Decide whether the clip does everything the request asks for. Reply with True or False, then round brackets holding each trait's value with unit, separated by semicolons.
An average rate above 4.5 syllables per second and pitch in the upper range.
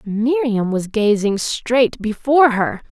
False (3.6 syllables/s; 230 Hz)